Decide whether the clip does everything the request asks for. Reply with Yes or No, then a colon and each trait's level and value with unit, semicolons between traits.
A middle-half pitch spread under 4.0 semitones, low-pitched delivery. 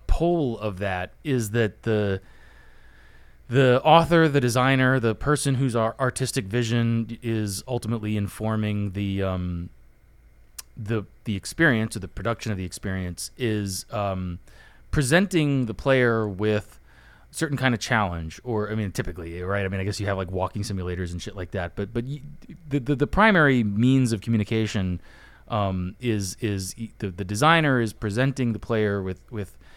No: average, 4.6 semitones; low, 110 Hz